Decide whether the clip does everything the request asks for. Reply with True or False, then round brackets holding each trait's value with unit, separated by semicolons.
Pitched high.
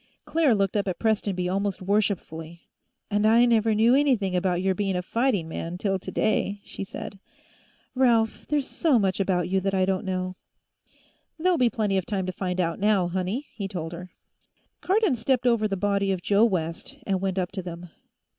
True (195 Hz)